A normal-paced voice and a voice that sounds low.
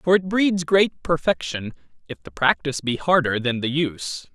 No: average, 180 wpm; medium, 150 Hz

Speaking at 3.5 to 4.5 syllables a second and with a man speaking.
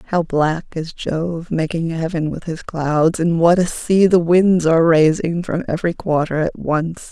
No: 4.3 syllables/s; female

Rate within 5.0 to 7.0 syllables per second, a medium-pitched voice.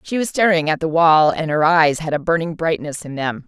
Yes: 5.3 syllables/s; medium, 160 Hz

